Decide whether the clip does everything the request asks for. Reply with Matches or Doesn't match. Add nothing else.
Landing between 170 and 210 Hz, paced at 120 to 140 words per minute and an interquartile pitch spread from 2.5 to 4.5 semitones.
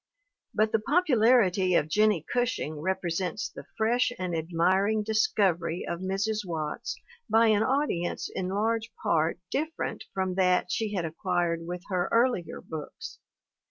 Matches